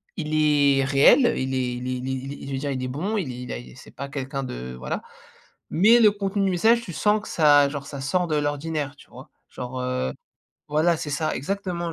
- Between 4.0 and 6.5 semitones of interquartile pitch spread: Yes, average, 4.6 semitones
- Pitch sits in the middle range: Yes, medium, 145 Hz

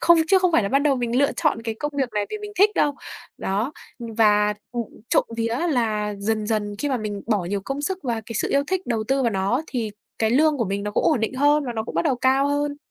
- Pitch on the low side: No, high, 240 Hz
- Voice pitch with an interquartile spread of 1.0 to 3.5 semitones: No, average, 5.2 semitones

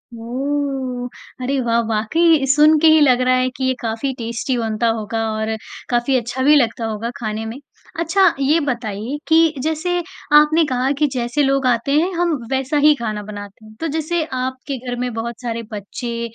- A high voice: Yes, very high, 255 Hz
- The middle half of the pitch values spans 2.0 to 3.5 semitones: No, average, 4.3 semitones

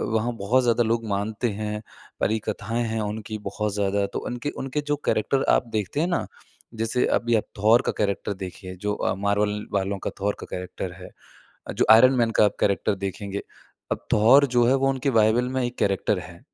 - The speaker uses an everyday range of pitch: Yes, average, 3.1 semitones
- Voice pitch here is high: No, low, 110 Hz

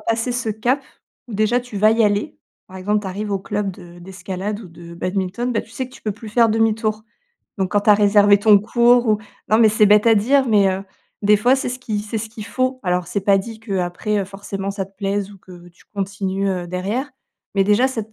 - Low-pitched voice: No, high, 205 Hz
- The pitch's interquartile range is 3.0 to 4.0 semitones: No, narrow, 2.5 semitones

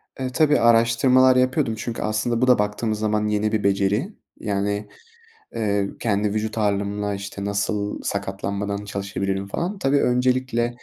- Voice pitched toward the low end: Yes, low, 105 Hz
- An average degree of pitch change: Yes, average, 3.3 semitones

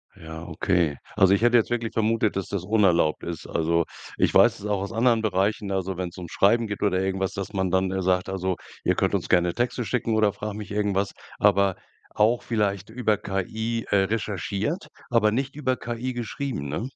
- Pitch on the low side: Yes, low, 100 Hz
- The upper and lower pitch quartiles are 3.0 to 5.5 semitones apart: Yes, average, 3.4 semitones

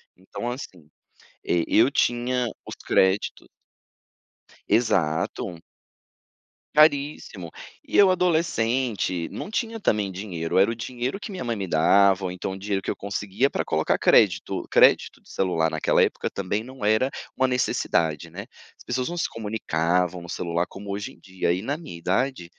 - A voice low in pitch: Yes, low, 100 Hz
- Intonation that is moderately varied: No, wide, 6.0 semitones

